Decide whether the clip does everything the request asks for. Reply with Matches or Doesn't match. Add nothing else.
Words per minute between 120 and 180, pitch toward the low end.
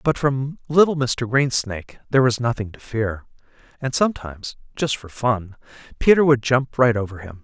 Matches